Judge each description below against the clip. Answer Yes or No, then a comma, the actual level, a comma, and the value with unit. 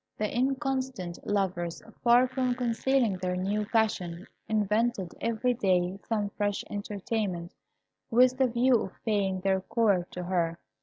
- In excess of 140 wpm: No, slow, 135 wpm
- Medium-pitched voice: No, high, 210 Hz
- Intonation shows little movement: No, average, 4.5 semitones